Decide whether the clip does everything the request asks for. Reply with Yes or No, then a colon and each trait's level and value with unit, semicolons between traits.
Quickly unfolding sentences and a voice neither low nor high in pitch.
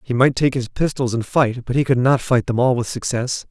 No: fast, 275 wpm; low, 125 Hz